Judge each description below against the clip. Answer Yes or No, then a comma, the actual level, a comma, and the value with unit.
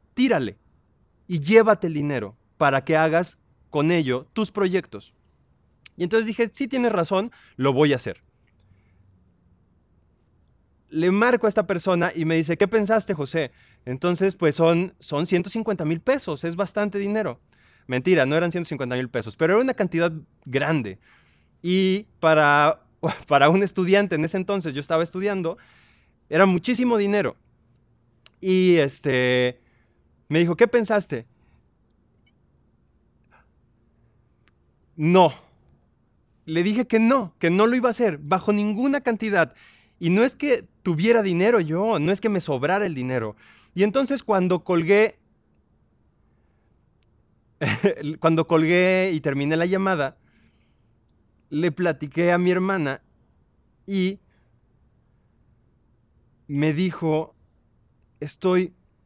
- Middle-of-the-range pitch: Yes, medium, 170 Hz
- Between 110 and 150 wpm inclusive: Yes, slow, 125 wpm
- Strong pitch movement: Yes, wide, 6.6 semitones